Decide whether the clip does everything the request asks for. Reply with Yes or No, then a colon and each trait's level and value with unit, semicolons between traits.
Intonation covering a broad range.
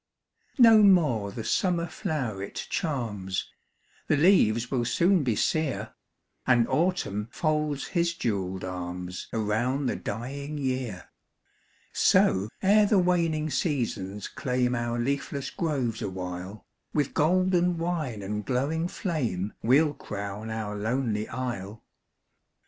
Yes: wide, 7.2 semitones